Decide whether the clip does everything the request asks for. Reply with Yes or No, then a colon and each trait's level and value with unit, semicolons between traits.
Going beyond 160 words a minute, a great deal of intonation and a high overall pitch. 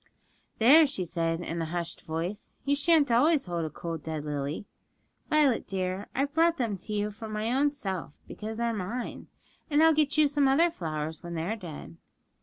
Yes: average, 195 wpm; wide, 9.0 semitones; high, 210 Hz